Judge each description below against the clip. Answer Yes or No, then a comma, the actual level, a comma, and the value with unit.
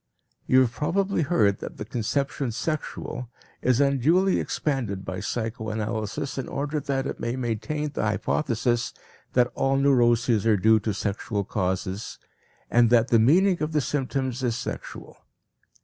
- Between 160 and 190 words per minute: No, average, 145 wpm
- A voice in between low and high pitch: No, low, 120 Hz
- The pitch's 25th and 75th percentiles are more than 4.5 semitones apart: No, average, 4.1 semitones